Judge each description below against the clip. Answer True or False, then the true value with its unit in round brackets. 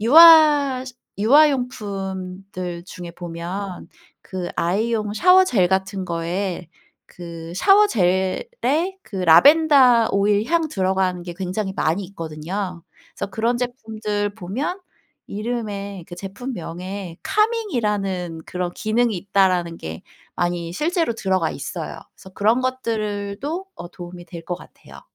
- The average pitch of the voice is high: True (200 Hz)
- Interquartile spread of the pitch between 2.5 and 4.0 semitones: False (5.2 semitones)